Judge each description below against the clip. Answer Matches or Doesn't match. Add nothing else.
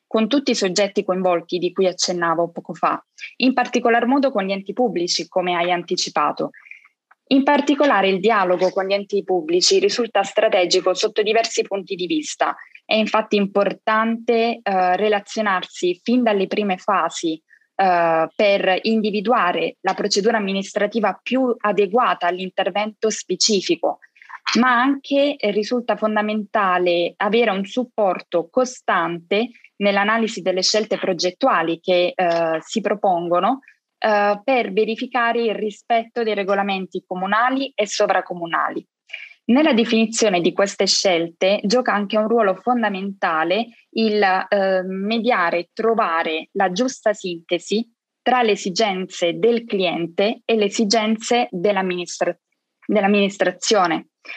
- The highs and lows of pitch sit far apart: Doesn't match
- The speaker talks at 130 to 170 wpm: Doesn't match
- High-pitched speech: Matches